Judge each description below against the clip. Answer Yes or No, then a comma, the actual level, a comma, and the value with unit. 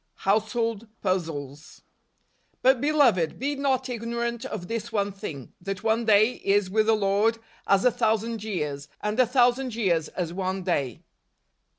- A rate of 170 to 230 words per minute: No, average, 155 wpm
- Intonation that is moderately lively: Yes, average, 4.0 semitones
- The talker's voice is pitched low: No, high, 215 Hz